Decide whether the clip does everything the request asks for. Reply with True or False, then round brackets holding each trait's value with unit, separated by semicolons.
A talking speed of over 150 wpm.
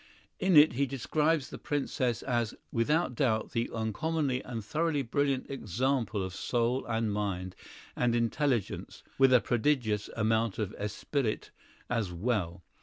False (135 wpm)